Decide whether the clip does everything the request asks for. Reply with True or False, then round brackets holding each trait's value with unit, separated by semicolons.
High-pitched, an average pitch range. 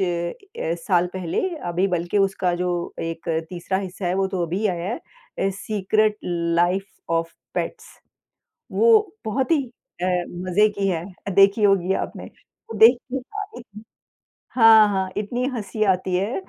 True (195 Hz; 3.3 semitones)